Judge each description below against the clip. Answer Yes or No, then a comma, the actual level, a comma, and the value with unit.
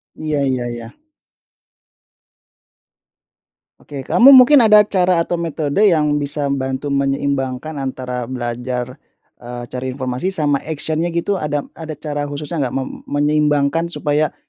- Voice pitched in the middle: Yes, medium, 145 Hz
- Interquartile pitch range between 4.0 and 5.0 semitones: No, average, 3.3 semitones